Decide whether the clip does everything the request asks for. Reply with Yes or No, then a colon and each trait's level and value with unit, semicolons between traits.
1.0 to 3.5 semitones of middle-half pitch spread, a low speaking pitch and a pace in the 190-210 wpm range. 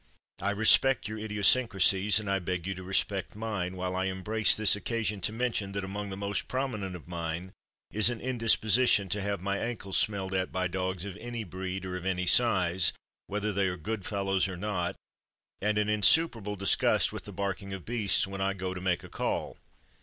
Yes: narrow, 2.4 semitones; low, 100 Hz; average, 200 wpm